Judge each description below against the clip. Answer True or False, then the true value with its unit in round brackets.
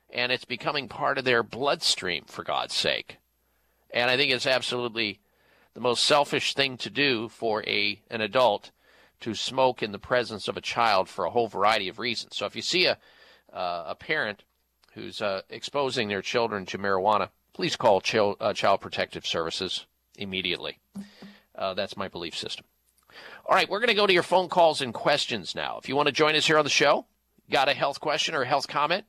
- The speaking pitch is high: False (125 Hz)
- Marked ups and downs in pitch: True (6.4 semitones)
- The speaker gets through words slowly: False (200 wpm)